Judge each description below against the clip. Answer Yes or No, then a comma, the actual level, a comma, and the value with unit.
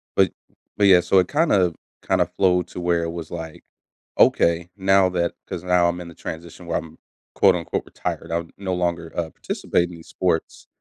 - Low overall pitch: Yes, very low, 85 Hz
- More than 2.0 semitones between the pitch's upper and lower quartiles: No, narrow, 1.7 semitones